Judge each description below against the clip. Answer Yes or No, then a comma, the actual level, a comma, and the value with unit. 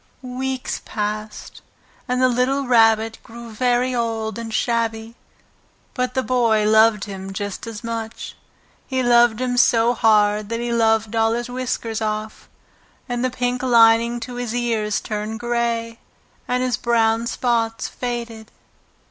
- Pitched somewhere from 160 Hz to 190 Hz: No, high, 230 Hz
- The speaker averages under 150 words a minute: Yes, average, 140 wpm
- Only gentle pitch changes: Yes, narrow, 1.7 semitones